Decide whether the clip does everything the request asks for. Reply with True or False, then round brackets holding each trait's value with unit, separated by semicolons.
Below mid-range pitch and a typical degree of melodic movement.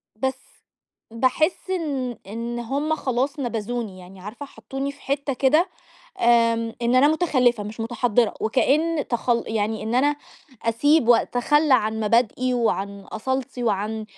False (245 Hz; 3.7 semitones)